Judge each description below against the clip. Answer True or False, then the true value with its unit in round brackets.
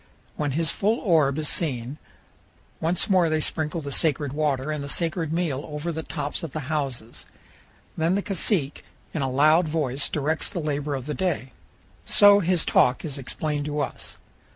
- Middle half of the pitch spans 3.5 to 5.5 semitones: False (2.7 semitones)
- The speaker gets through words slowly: False (175 wpm)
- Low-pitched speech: False (150 Hz)